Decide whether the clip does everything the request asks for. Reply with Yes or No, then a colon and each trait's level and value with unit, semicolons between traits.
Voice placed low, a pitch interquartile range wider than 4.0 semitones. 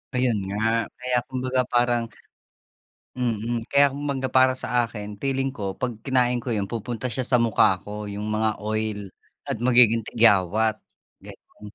No: low, 115 Hz; average, 3.0 semitones